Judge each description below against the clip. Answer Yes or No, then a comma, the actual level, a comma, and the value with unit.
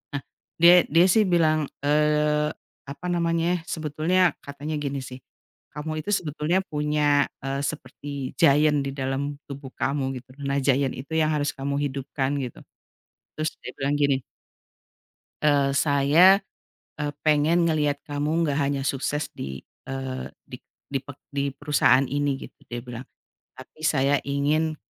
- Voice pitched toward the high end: No, medium, 145 Hz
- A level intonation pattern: Yes, narrow, 2.0 semitones